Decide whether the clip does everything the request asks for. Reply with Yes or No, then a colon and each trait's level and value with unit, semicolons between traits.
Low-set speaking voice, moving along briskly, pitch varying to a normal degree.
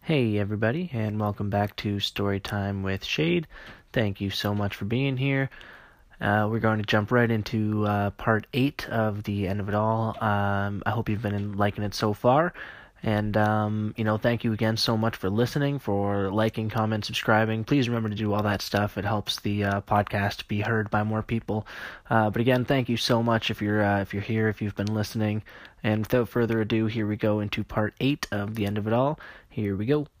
No: low, 110 Hz; fast, 215 wpm; narrow, 1.9 semitones